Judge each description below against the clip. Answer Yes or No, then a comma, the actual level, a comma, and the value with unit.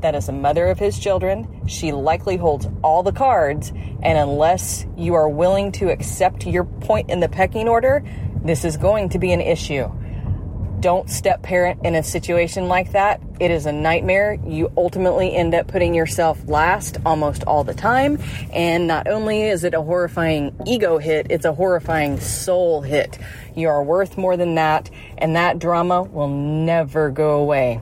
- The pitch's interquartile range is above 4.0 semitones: No, average, 3.2 semitones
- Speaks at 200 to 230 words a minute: No, average, 180 wpm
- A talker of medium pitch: Yes, medium, 165 Hz